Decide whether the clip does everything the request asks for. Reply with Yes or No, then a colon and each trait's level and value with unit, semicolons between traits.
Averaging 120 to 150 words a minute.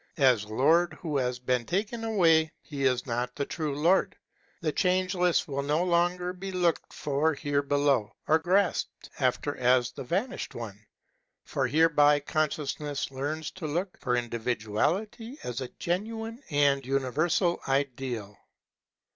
Yes: average, 140 wpm